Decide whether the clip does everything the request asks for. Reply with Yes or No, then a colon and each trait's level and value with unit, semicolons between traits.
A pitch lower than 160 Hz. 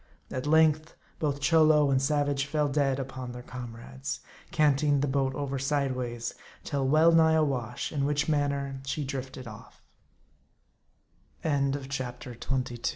Yes: medium, 140 Hz